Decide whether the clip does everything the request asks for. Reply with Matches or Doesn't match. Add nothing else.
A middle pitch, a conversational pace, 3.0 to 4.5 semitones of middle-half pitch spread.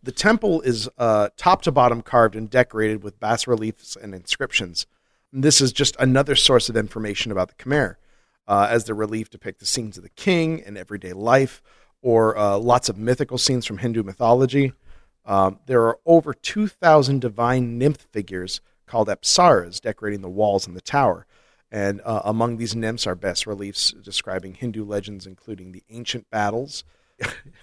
Doesn't match